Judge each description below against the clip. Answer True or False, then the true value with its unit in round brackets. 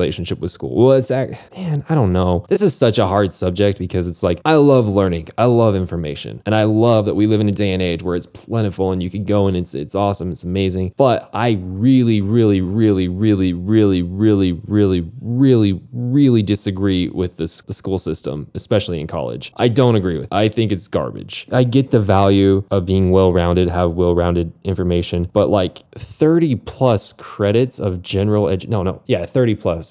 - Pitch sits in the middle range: False (100 Hz)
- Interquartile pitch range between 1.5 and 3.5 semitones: False (4.0 semitones)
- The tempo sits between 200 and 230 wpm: True (205 wpm)